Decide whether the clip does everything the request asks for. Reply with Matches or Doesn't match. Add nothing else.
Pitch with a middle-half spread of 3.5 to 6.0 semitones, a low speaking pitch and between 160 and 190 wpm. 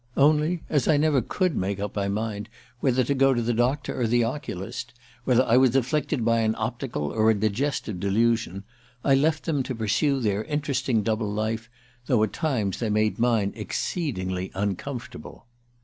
Matches